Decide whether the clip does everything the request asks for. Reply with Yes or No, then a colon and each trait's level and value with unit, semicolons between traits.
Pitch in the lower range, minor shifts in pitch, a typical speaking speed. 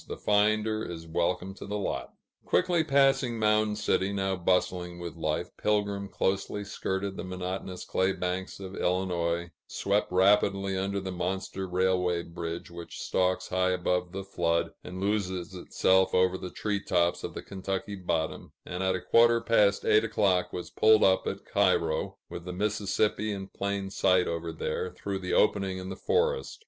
Yes: very low, 95 Hz; narrow, 2.1 semitones; average, 165 wpm